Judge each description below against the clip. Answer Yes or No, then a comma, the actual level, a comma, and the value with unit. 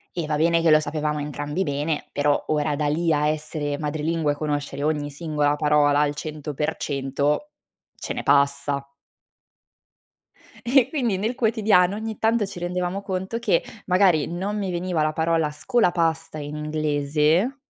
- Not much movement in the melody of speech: No, average, 3.6 semitones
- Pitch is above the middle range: No, medium, 155 Hz